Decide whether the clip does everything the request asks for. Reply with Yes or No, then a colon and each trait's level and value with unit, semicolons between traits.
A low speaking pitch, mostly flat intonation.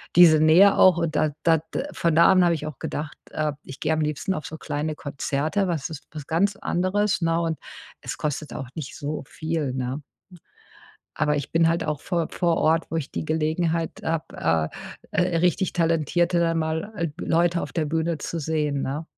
No: medium, 160 Hz; narrow, 2.0 semitones